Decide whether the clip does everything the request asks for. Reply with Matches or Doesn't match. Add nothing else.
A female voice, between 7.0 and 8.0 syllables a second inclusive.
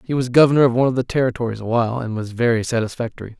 Doesn't match